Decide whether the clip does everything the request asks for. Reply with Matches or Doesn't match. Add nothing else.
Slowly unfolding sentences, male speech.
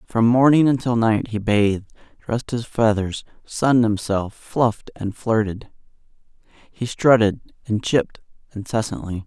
Matches